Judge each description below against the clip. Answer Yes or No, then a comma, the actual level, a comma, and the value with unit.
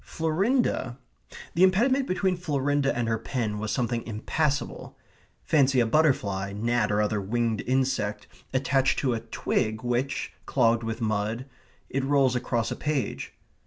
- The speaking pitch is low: Yes, low, 125 Hz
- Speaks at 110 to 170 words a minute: Yes, average, 140 wpm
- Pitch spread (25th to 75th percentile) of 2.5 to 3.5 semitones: No, average, 4.4 semitones